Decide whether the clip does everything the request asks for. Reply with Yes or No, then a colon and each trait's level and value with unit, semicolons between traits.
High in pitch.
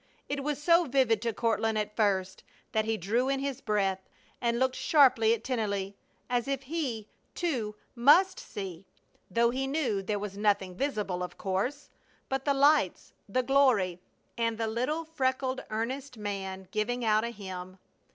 Yes: high, 230 Hz